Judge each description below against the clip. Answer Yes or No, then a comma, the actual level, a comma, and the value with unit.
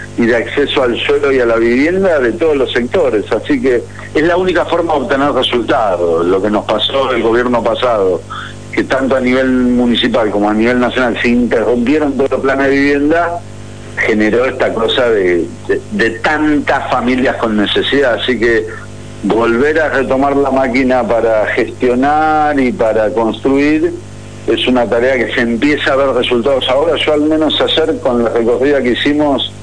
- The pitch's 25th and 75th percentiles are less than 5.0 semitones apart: Yes, average, 4.3 semitones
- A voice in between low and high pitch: No, low, 130 Hz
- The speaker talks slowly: No, average, 175 wpm